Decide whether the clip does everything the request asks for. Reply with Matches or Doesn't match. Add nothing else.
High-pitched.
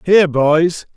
Doesn't match